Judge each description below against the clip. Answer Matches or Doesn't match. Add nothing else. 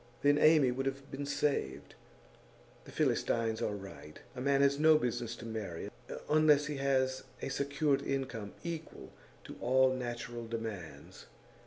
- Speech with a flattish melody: Doesn't match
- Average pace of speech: Matches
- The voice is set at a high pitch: Doesn't match